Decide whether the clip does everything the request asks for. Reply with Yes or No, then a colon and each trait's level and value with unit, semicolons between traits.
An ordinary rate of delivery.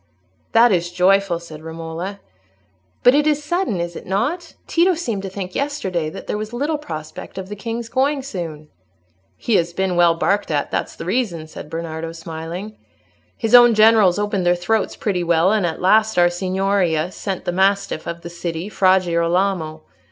Yes: average, 180 wpm